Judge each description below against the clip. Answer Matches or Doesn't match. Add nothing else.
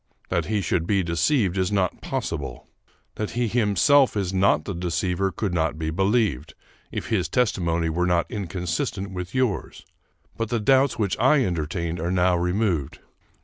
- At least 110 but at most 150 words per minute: Doesn't match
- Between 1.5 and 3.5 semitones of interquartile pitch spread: Doesn't match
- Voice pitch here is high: Doesn't match